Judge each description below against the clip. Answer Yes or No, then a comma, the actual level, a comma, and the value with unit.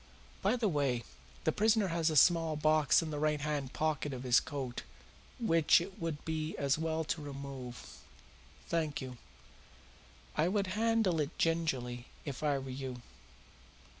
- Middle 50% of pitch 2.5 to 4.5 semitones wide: Yes, average, 3.4 semitones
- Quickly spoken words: No, average, 155 wpm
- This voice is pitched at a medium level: Yes, medium, 155 Hz